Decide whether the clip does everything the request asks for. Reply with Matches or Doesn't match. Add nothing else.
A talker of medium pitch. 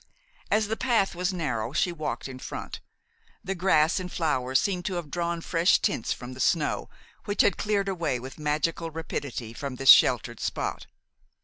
Matches